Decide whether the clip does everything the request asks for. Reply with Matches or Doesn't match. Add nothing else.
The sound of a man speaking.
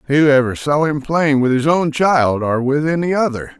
Matches